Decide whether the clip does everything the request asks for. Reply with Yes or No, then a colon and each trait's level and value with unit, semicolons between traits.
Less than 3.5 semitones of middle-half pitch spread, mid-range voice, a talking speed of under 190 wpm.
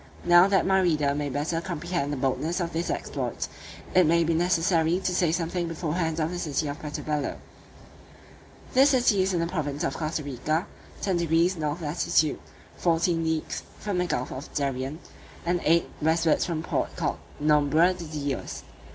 Yes: average, 2.7 semitones; medium, 165 Hz; average, 175 wpm